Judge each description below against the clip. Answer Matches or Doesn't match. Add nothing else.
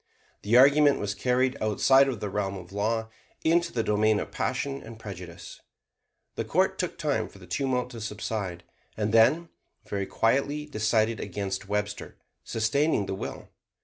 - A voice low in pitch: Matches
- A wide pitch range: Doesn't match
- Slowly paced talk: Doesn't match